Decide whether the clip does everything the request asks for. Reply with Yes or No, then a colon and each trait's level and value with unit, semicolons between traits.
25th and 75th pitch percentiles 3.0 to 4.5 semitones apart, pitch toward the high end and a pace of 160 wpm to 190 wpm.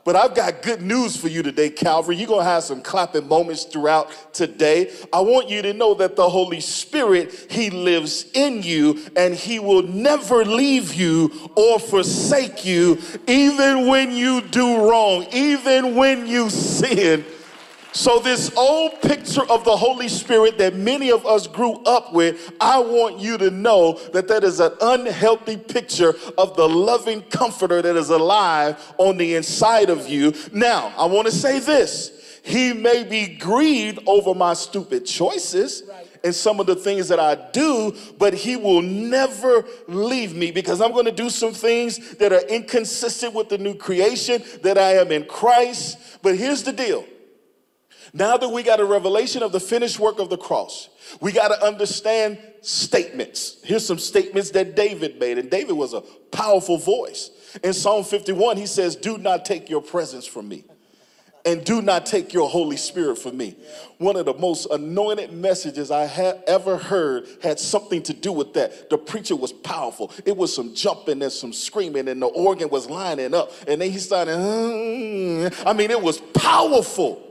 No: average, 5.3 semitones; high, 205 Hz; average, 180 wpm